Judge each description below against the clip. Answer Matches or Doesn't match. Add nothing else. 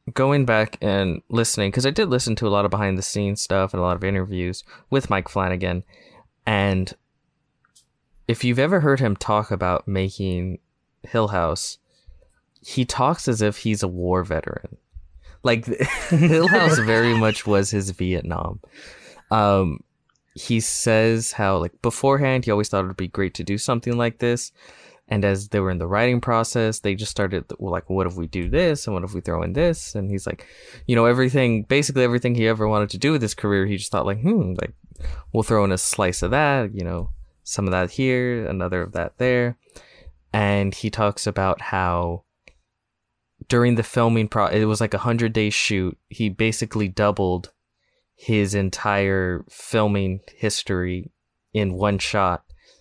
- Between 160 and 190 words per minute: Matches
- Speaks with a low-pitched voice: Matches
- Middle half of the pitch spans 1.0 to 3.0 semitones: Doesn't match